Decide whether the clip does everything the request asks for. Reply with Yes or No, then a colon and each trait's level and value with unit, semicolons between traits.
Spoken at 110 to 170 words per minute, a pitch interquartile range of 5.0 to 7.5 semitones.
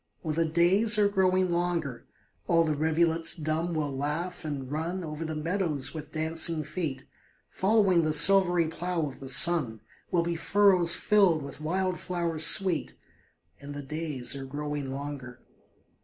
No: average, 155 wpm; average, 3.1 semitones